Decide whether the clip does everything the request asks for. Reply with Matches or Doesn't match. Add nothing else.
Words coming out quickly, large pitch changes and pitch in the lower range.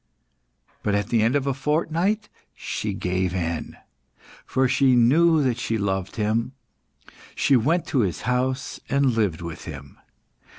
Doesn't match